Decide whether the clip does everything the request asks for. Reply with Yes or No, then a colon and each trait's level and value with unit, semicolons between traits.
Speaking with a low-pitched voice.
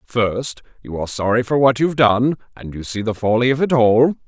Yes: low, 120 Hz